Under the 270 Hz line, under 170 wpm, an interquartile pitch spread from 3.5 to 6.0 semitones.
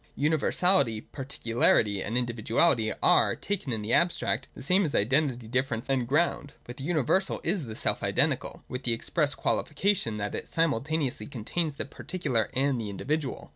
Yes: low, 135 Hz; average, 160 wpm; wide, 5.4 semitones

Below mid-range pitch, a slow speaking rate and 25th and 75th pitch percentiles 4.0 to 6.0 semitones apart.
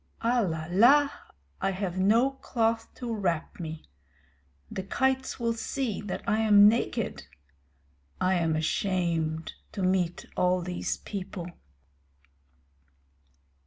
No: high, 195 Hz; slow, 105 wpm; average, 4.6 semitones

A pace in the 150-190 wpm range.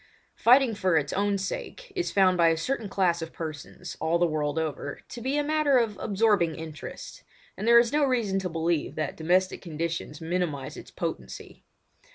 Yes: average, 185 wpm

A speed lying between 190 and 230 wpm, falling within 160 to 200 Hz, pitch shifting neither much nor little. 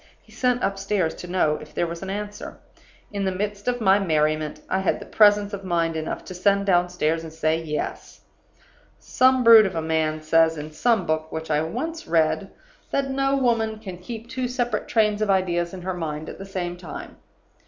Yes: average, 195 wpm; medium, 185 Hz; average, 4.8 semitones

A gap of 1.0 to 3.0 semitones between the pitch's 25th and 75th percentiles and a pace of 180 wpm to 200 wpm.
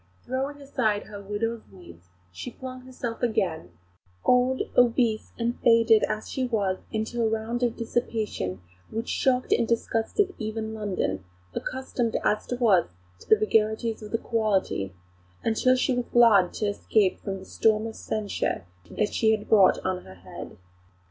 No: average, 2.7 semitones; average, 155 wpm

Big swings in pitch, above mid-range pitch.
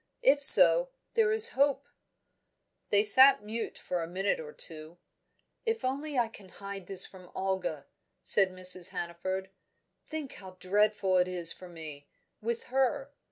Yes: wide, 6.6 semitones; high, 195 Hz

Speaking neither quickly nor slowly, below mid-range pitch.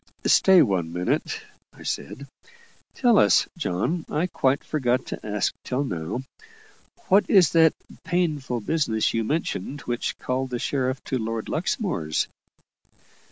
No: slow, 130 wpm; low, 130 Hz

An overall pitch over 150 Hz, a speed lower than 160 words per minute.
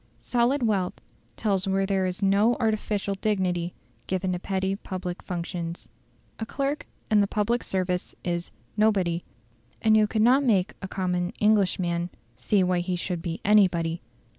Yes: high, 190 Hz; average, 150 wpm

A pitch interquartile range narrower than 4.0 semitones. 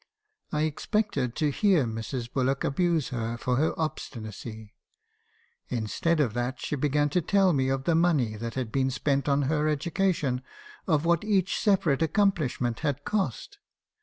No: average, 5.0 semitones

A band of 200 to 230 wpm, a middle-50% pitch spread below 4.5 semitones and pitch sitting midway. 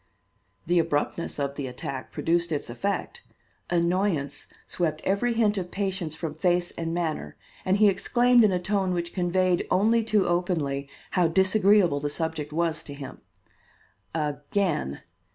No: average, 145 wpm; average, 4.1 semitones; medium, 175 Hz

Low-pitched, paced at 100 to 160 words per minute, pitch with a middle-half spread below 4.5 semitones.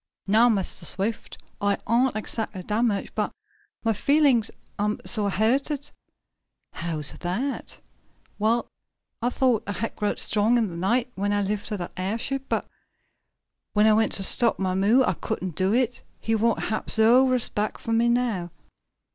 No: high, 220 Hz; average, 155 wpm; average, 3.2 semitones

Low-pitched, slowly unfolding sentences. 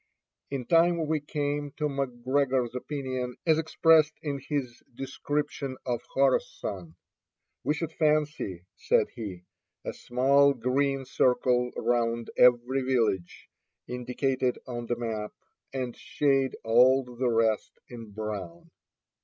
Yes: low, 130 Hz; slow, 115 wpm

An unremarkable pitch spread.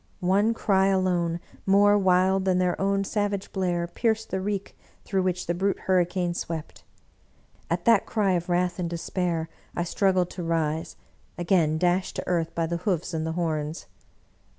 No: narrow, 2.1 semitones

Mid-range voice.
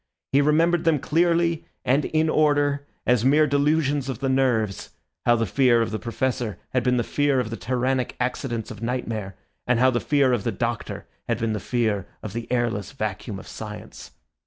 No: low, 125 Hz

